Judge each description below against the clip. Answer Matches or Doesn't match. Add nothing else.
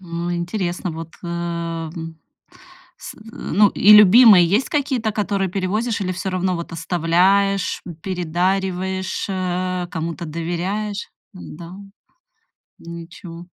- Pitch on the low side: Doesn't match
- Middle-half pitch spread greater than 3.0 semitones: Doesn't match